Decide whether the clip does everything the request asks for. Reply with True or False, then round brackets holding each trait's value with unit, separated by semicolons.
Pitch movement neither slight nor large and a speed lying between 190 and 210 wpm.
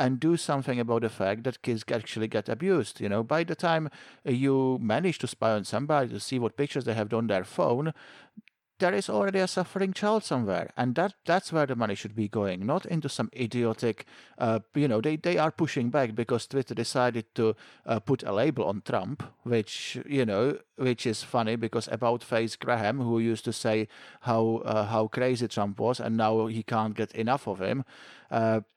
True (3.9 semitones; 205 wpm)